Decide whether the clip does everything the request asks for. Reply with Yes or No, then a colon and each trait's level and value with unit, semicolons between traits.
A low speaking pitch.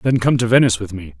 Yes: low, 110 Hz